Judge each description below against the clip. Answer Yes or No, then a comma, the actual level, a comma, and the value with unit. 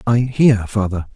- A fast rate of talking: No, average, 155 wpm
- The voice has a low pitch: Yes, low, 110 Hz